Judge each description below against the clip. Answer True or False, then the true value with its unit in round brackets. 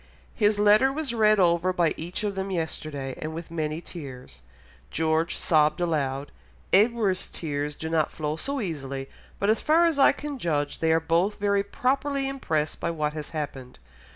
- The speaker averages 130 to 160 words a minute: False (175 wpm)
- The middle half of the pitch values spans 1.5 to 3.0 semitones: False (5.5 semitones)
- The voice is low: False (170 Hz)